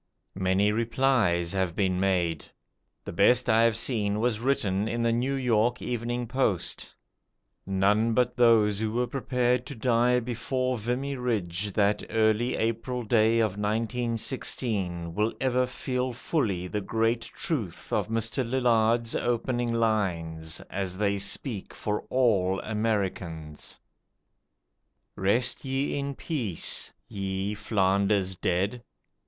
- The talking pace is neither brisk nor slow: No, slow, 125 wpm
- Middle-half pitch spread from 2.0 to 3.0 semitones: No, average, 3.9 semitones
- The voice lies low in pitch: Yes, low, 110 Hz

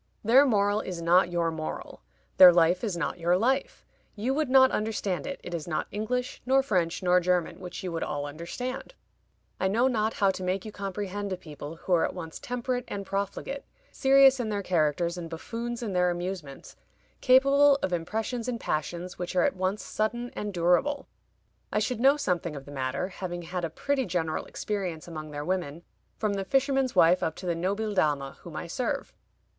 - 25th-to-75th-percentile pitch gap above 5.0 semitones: Yes, wide, 5.5 semitones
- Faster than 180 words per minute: Yes, average, 195 wpm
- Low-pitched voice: No, high, 190 Hz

